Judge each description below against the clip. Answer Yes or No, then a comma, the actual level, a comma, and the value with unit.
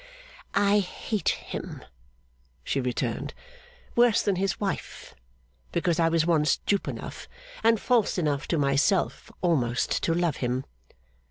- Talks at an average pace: No, slow, 125 wpm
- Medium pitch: Yes, medium, 170 Hz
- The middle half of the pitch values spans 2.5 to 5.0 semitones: No, wide, 5.5 semitones